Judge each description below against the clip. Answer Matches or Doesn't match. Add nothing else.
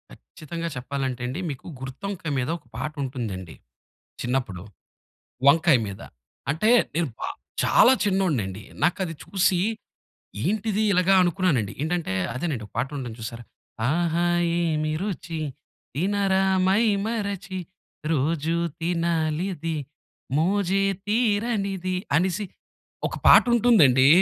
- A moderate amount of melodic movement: Doesn't match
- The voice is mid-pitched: Matches